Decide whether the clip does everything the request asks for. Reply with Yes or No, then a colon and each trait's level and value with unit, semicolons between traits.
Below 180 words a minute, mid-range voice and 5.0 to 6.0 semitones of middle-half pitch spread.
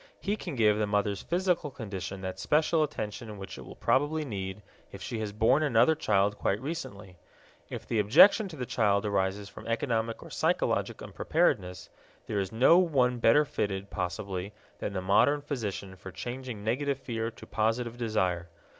No: average, 170 wpm; low, 110 Hz; average, 5.3 semitones